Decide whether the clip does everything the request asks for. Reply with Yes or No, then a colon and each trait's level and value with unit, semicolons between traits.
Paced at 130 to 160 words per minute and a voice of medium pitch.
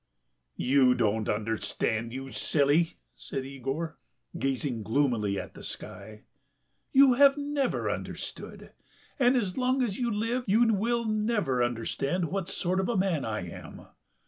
Yes: slow, 135 wpm; medium, 160 Hz